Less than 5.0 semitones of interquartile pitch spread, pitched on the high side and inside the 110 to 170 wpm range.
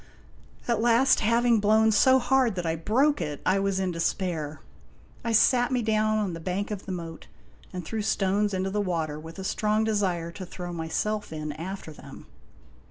No: average, 4.4 semitones; high, 195 Hz; average, 185 wpm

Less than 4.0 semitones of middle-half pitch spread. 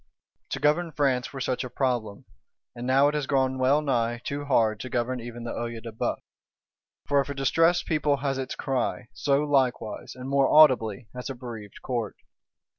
Yes: average, 3.0 semitones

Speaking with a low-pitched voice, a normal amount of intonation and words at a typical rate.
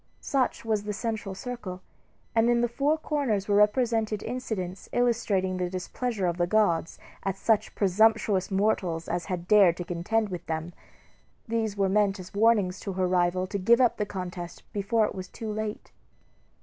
No: high, 205 Hz; average, 3.4 semitones; average, 175 wpm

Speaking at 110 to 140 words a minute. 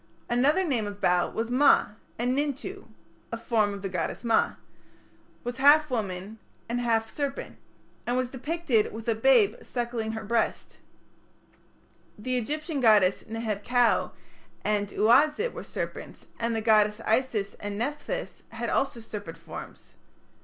No: average, 155 wpm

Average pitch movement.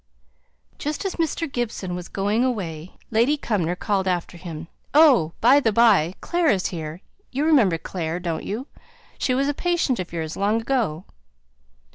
No: wide, 7.4 semitones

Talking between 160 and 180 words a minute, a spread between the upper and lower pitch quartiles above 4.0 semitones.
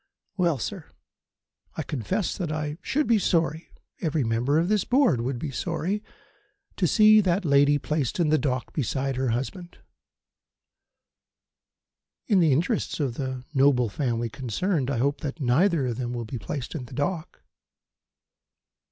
No: average, 150 wpm; average, 5.3 semitones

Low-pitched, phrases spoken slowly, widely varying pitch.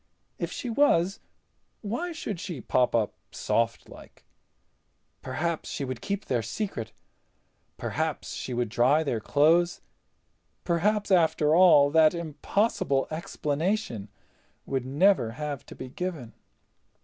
No: medium, 155 Hz; slow, 115 wpm; wide, 6.4 semitones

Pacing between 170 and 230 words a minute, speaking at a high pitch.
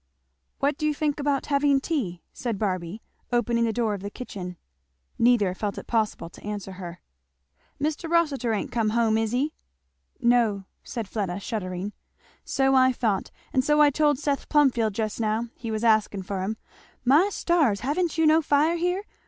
Yes: average, 175 wpm; high, 235 Hz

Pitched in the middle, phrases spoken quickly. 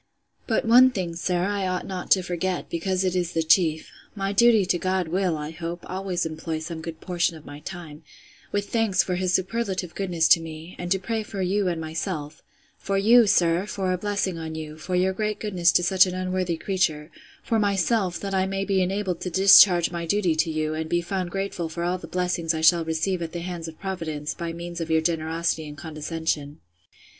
Yes: medium, 180 Hz; fast, 215 wpm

